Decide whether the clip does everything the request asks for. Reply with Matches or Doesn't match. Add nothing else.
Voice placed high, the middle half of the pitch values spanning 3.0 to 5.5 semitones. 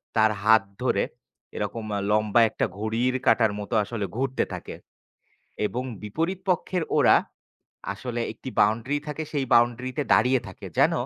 Doesn't match